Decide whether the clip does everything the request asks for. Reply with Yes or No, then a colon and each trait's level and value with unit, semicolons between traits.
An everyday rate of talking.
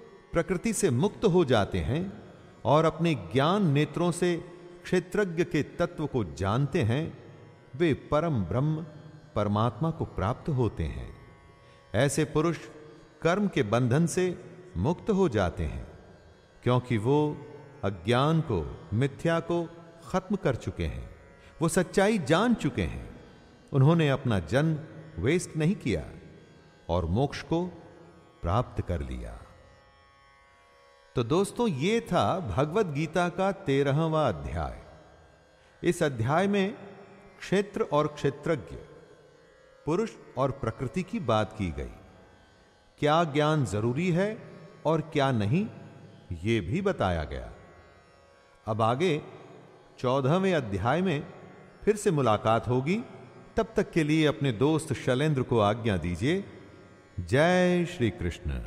No: slow, 120 wpm